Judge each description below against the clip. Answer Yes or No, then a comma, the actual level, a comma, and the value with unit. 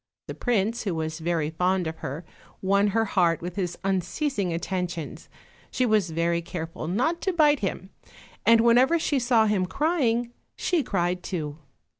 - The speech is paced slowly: No, average, 160 wpm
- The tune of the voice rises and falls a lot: Yes, wide, 5.7 semitones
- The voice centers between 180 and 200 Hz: Yes, high, 190 Hz